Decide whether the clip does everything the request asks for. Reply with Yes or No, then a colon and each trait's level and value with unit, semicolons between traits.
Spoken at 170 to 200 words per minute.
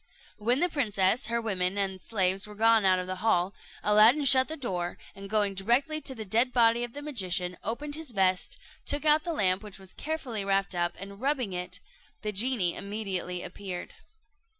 Yes: average, 190 wpm